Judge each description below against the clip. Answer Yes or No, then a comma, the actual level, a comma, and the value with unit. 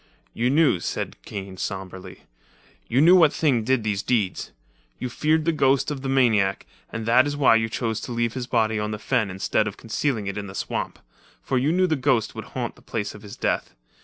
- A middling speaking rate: No, fast, 220 wpm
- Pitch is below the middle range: Yes, low, 115 Hz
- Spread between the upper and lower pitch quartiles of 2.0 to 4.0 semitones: No, average, 4.4 semitones